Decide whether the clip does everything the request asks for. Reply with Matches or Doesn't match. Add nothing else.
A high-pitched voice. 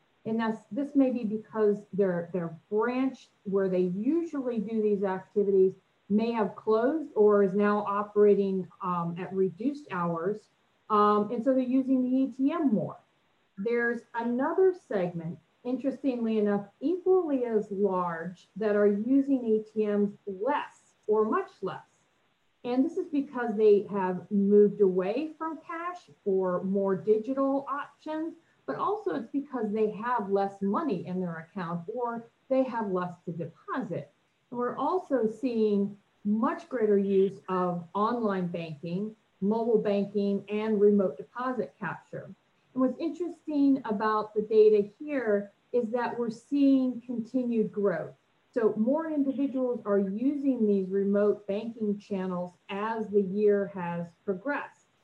Matches